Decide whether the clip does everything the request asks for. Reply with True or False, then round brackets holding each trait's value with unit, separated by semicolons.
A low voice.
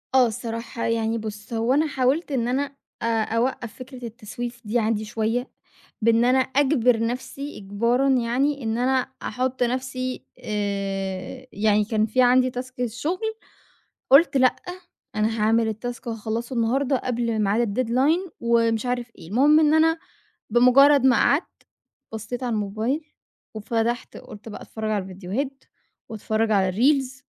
False (240 Hz)